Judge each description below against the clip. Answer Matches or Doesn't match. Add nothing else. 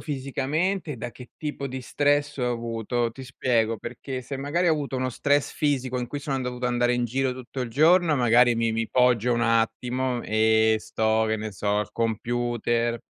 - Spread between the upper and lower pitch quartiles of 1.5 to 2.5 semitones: Doesn't match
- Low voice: Matches